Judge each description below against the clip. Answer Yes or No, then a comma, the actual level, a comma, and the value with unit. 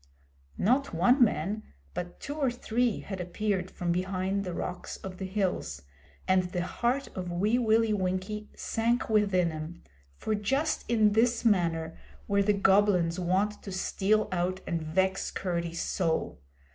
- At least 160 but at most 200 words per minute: No, average, 150 wpm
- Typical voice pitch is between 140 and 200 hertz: Yes, high, 190 Hz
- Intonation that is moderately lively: Yes, average, 3.3 semitones